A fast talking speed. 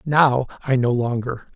No: average, 155 wpm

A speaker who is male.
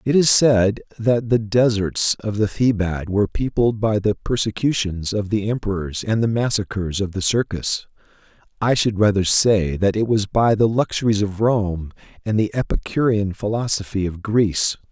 Yes: male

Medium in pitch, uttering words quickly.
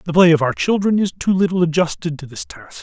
Yes: medium, 170 Hz; fast, 255 wpm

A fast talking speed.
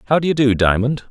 Yes: fast, 270 wpm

